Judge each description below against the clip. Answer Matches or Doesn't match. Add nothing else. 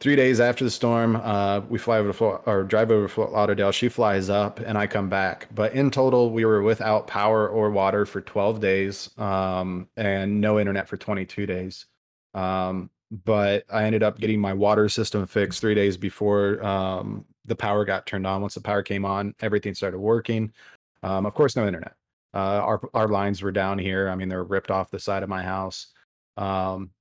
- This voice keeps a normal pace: Doesn't match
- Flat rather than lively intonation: Matches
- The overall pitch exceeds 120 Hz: Doesn't match